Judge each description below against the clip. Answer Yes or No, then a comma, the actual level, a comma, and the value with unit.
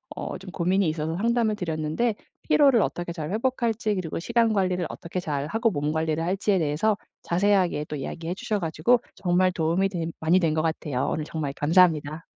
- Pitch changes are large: No, average, 4.5 semitones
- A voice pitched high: No, medium, 175 Hz